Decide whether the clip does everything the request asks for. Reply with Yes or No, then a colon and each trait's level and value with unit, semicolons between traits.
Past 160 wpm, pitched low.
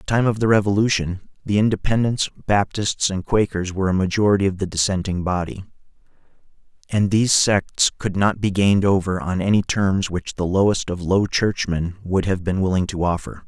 Yes: average, 185 wpm; very low, 95 Hz